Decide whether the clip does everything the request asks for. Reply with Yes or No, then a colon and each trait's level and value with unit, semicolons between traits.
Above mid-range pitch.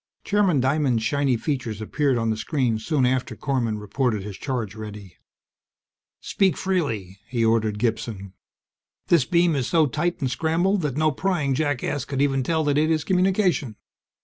No: low, 135 Hz